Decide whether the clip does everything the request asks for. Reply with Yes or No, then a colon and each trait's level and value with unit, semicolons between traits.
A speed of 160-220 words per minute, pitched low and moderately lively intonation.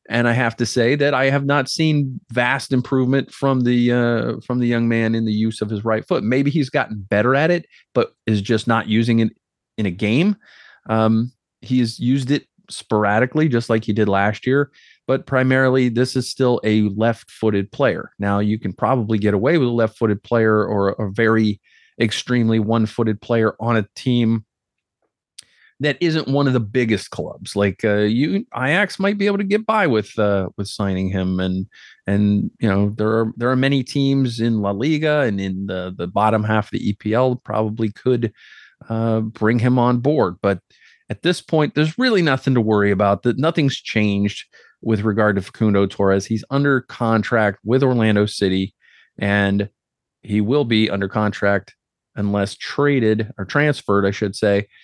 Yes: average, 185 wpm; low, 115 Hz; average, 3.8 semitones